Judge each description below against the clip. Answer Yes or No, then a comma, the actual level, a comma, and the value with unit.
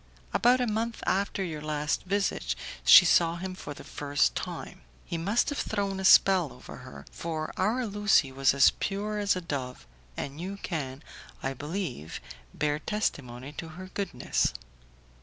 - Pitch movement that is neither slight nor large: No, wide, 5.8 semitones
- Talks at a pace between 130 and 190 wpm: Yes, average, 160 wpm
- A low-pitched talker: No, medium, 170 Hz